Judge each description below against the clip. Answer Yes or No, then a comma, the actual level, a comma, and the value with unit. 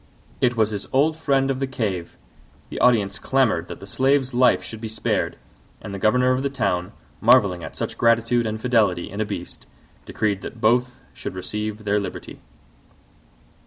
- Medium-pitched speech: No, low, 110 Hz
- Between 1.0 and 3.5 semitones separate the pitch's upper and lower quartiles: No, average, 4.0 semitones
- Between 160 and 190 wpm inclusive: Yes, average, 175 wpm